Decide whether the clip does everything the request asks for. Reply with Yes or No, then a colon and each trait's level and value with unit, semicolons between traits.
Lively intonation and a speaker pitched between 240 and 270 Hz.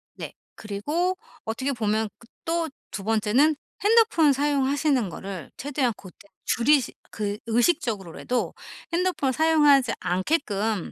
Yes: wide, 6.1 semitones; very high, 255 Hz